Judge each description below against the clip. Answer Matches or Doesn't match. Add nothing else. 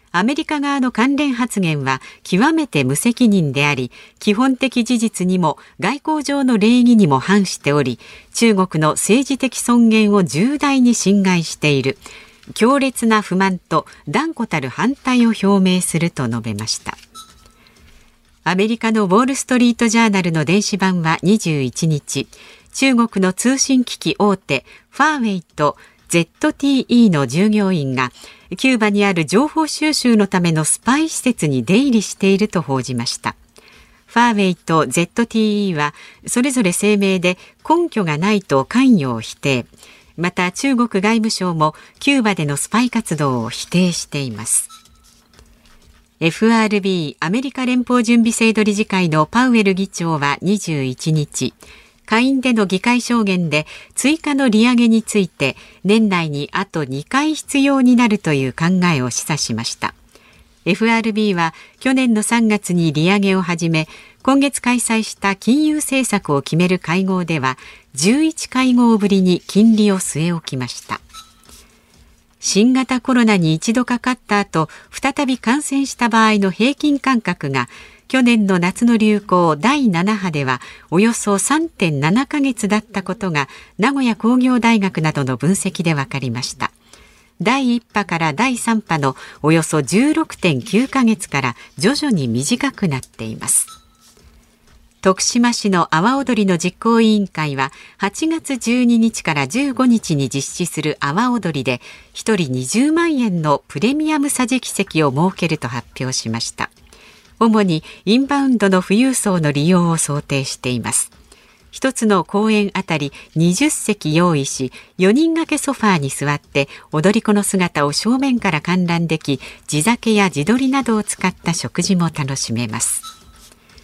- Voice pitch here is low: Doesn't match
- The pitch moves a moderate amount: Doesn't match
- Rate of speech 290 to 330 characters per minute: Doesn't match